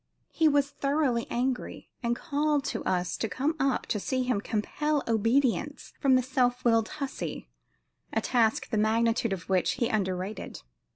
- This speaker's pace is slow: No, average, 160 wpm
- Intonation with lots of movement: No, average, 4.0 semitones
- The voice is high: Yes, high, 245 Hz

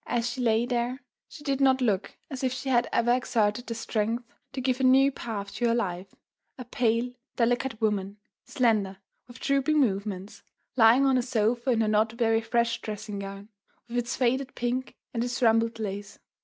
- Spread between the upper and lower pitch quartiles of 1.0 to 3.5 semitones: Yes, average, 2.8 semitones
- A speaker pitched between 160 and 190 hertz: No, high, 235 Hz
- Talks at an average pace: Yes, average, 185 wpm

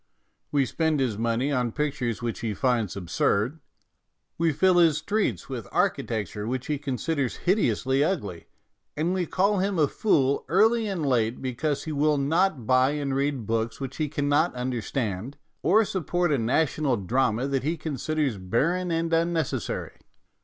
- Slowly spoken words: No, average, 160 wpm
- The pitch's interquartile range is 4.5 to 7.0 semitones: Yes, average, 5.1 semitones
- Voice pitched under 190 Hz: Yes, medium, 140 Hz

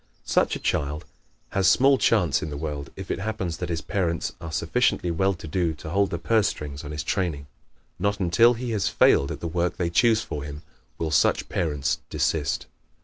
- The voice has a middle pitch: No, very low, 85 Hz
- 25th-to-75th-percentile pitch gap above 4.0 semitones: Yes, average, 4.4 semitones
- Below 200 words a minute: No, fast, 205 wpm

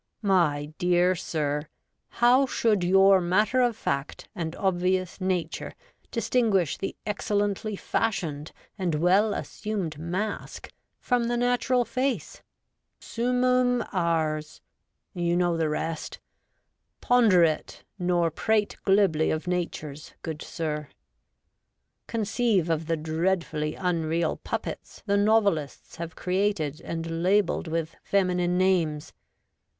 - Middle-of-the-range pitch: Yes, medium, 180 Hz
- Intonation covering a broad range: No, average, 4.4 semitones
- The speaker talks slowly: Yes, slow, 110 wpm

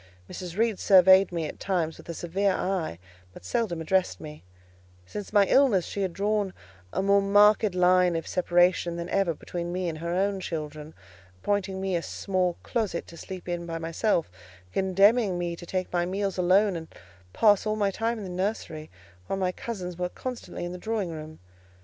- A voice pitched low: No, medium, 185 Hz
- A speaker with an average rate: Yes, average, 185 wpm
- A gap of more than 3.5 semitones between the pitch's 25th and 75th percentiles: No, average, 2.7 semitones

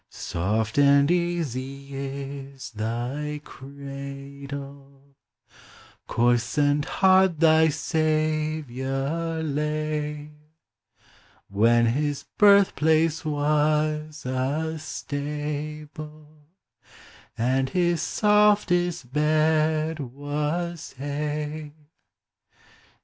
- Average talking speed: No, slow, 65 wpm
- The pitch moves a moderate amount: No, narrow, 2.2 semitones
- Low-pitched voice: No, medium, 150 Hz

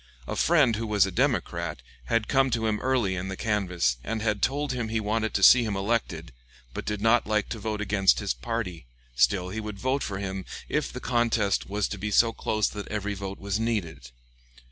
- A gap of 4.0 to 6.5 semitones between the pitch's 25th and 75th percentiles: No, average, 2.7 semitones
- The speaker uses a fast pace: Yes, fast, 210 wpm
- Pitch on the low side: Yes, low, 105 Hz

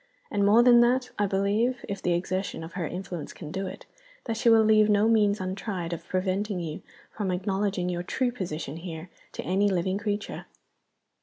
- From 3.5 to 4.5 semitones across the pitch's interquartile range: No, average, 3.0 semitones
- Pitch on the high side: Yes, high, 195 Hz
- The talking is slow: No, average, 185 wpm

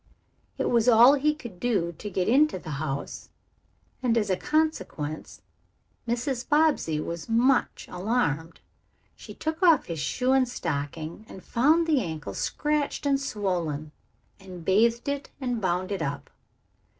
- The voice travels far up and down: Yes, wide, 8.3 semitones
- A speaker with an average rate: Yes, average, 145 wpm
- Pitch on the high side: Yes, high, 225 Hz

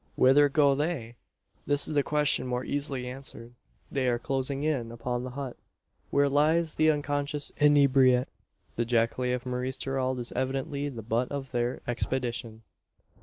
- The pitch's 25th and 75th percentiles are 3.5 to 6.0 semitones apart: No, narrow, 2.6 semitones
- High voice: No, low, 130 Hz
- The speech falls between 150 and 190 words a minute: Yes, average, 155 wpm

